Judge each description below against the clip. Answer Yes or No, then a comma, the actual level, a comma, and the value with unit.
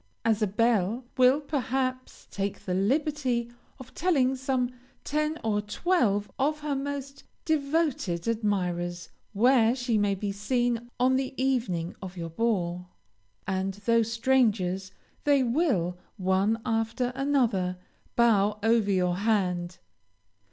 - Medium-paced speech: No, slow, 125 wpm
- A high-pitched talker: Yes, high, 230 Hz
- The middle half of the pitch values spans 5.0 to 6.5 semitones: Yes, average, 5.3 semitones